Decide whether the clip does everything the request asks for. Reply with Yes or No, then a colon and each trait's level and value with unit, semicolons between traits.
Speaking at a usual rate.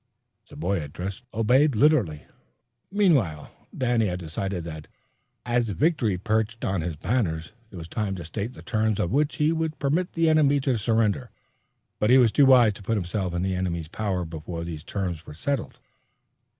Yes: average, 175 wpm